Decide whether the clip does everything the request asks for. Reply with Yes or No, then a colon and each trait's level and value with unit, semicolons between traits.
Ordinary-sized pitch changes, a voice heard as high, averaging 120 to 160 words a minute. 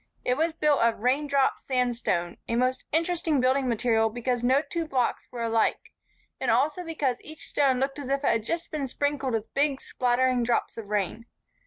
No: average, 3.5 semitones; very high, 255 Hz; average, 185 wpm